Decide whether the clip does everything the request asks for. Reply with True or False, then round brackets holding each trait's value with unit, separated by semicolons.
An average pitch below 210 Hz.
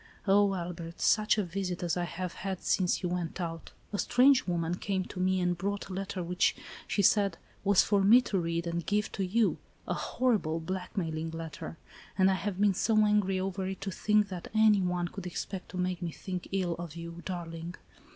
True (185 Hz)